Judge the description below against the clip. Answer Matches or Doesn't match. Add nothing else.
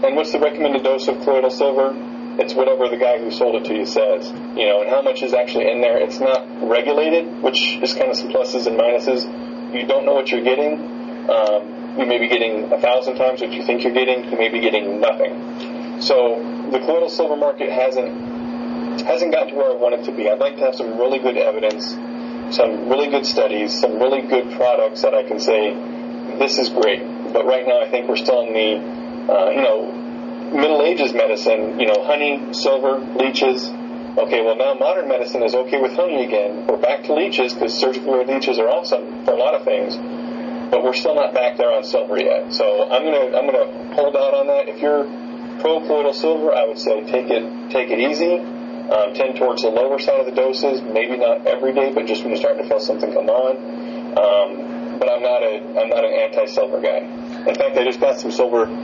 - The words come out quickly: Matches